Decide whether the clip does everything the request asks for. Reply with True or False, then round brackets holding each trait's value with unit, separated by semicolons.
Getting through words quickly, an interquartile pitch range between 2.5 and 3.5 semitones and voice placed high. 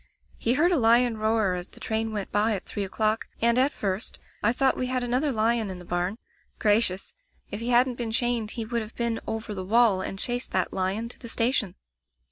True (220 wpm; 2.8 semitones; 225 Hz)